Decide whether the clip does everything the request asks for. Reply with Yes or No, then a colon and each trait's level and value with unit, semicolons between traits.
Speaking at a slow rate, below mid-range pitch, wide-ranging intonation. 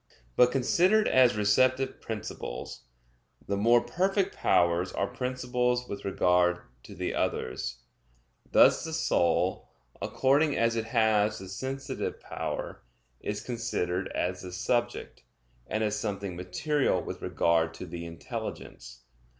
Yes: slow, 125 wpm; low, 110 Hz; wide, 5.9 semitones